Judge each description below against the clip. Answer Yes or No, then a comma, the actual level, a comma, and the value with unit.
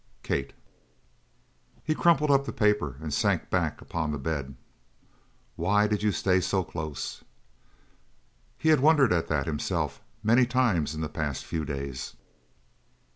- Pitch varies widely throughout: Yes, wide, 8.1 semitones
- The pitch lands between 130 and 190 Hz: No, very low, 90 Hz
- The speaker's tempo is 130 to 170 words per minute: Yes, average, 140 wpm